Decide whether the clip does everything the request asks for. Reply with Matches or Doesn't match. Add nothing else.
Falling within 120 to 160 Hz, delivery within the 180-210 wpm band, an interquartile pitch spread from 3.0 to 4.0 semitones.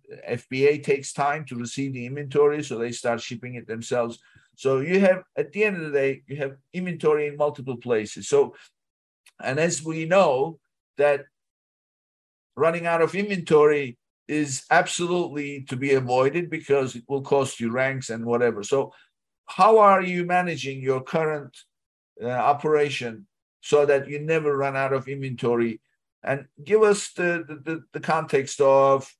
Doesn't match